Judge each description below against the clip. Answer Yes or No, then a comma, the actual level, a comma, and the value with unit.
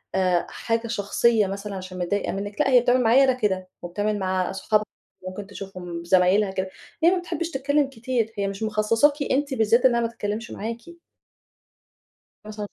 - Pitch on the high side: Yes, high, 215 Hz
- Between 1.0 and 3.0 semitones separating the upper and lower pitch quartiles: No, average, 4.2 semitones